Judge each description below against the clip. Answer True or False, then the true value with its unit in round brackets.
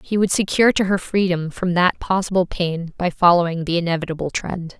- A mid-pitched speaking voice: True (180 Hz)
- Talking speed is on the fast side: False (190 wpm)